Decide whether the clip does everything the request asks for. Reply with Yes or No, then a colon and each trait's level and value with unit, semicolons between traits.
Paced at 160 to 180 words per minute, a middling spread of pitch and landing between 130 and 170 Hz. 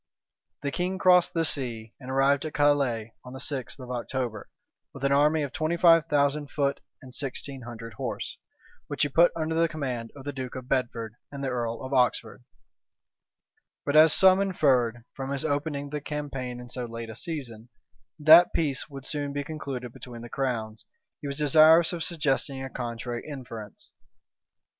Yes: average, 175 wpm; average, 3.5 semitones; medium, 140 Hz